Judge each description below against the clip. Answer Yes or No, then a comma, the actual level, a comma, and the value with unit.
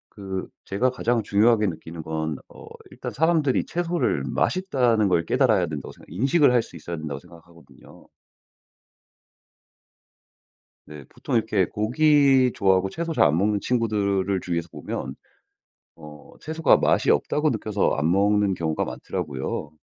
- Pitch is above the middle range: No, low, 100 Hz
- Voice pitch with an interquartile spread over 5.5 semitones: Yes, wide, 7.0 semitones